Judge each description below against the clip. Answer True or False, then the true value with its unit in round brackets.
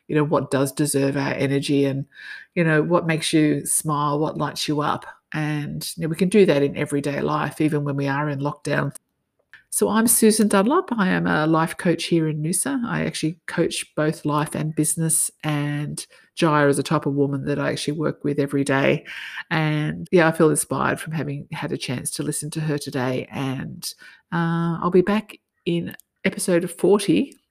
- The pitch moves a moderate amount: True (3.0 semitones)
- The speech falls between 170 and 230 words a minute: True (195 wpm)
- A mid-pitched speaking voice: True (155 Hz)